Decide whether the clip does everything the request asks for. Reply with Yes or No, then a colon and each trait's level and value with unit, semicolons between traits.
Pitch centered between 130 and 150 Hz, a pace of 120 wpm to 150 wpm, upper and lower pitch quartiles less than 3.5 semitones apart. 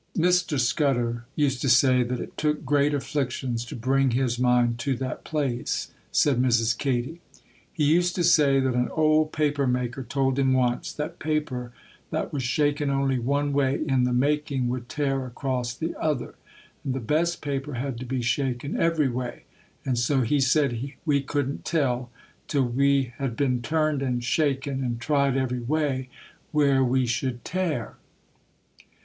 No: low, 135 Hz; average, 165 wpm; average, 2.8 semitones